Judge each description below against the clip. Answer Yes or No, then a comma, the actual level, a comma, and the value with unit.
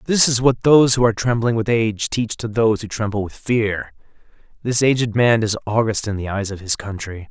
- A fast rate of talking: Yes, fast, 220 wpm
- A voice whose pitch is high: No, low, 110 Hz